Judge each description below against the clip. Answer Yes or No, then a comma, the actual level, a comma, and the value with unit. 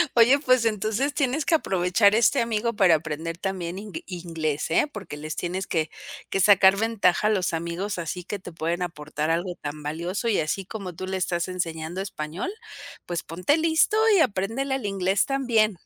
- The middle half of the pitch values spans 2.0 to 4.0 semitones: No, average, 4.7 semitones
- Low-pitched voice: No, high, 190 Hz